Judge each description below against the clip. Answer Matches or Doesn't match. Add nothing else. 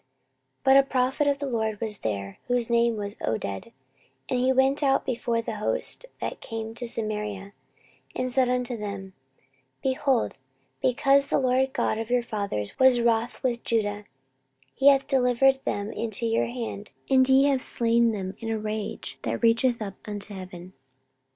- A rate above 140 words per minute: Matches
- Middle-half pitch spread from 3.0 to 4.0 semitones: Matches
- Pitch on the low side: Doesn't match